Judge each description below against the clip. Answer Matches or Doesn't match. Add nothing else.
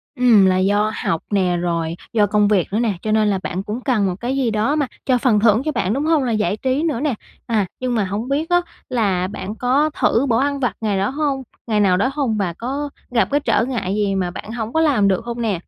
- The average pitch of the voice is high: Matches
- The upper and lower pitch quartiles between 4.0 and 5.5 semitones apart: Matches